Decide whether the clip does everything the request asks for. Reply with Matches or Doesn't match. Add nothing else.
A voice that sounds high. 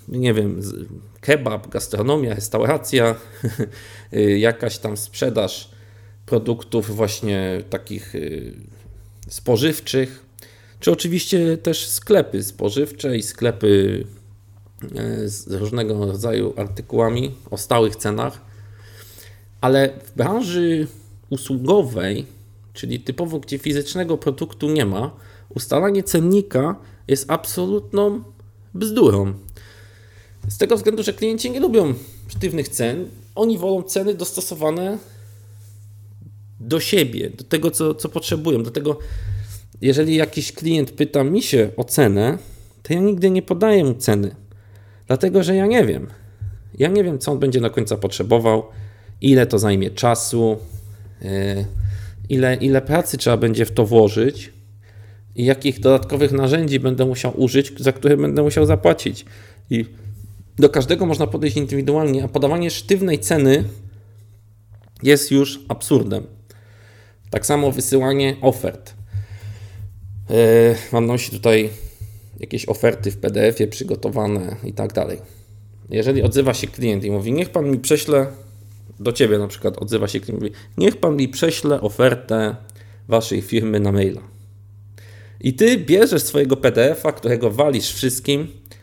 Doesn't match